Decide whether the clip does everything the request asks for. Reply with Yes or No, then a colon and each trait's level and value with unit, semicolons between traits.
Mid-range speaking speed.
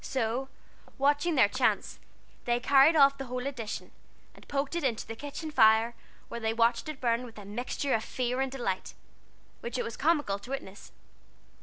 Yes: average, 180 wpm